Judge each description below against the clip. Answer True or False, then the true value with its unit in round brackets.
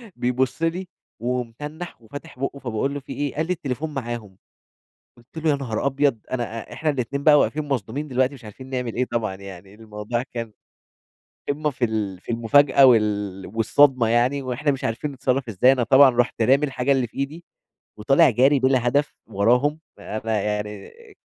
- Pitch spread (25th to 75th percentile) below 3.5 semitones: False (3.9 semitones)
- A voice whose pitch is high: False (125 Hz)